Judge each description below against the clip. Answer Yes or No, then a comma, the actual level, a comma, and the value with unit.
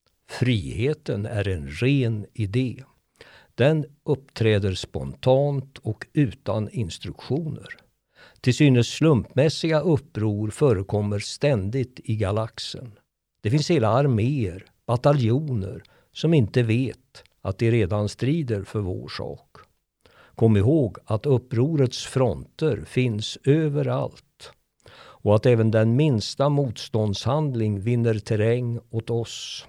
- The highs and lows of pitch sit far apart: No, average, 4.3 semitones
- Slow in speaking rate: Yes, slow, 105 wpm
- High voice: No, low, 120 Hz